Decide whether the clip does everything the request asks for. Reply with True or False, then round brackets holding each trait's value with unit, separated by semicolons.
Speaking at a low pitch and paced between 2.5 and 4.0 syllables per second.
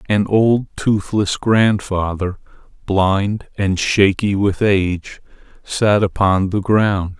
True (100 Hz; 3.2 syllables/s)